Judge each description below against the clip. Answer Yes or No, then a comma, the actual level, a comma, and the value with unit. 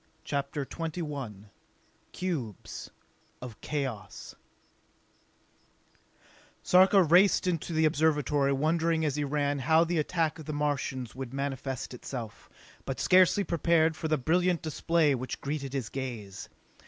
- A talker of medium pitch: Yes, medium, 150 Hz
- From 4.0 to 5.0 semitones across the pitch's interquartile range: No, average, 3.5 semitones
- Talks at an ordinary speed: No, slow, 120 wpm